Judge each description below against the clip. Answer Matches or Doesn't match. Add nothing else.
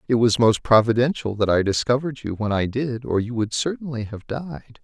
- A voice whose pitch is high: Doesn't match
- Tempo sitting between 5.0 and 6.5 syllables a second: Matches